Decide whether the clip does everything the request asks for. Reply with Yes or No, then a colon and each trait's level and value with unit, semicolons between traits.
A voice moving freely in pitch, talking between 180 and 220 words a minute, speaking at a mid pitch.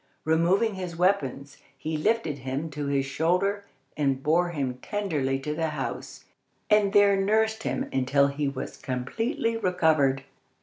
No: wide, 6.2 semitones; average, 140 wpm; medium, 160 Hz